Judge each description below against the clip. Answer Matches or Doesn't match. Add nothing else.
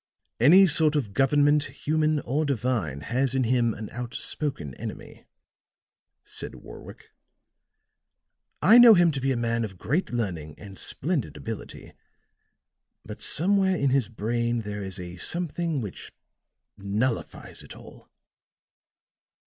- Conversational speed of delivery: Doesn't match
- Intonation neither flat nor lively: Doesn't match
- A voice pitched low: Matches